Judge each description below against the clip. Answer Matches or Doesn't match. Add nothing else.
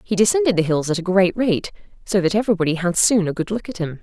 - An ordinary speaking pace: Doesn't match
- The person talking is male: Doesn't match